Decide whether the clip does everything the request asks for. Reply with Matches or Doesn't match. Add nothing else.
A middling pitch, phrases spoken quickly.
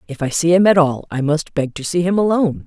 Matches